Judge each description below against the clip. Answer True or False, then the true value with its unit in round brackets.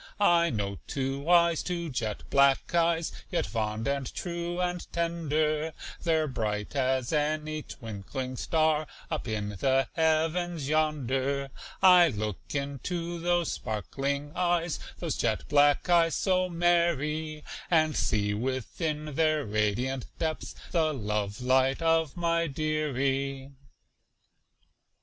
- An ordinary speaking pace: False (115 wpm)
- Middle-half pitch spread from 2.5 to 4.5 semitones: True (4.1 semitones)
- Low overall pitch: False (150 Hz)